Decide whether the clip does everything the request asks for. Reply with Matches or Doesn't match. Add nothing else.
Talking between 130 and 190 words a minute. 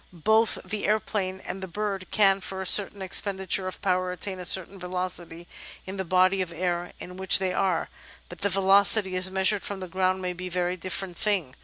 Doesn't match